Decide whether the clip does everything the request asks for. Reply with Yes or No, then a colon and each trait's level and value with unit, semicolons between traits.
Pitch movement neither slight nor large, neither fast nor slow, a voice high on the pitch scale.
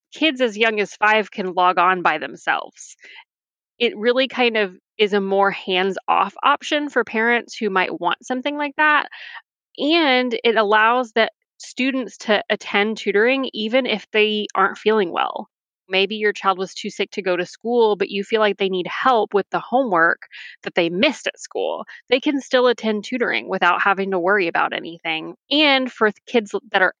Yes: average, 4.4 semitones; average, 185 wpm; high, 215 Hz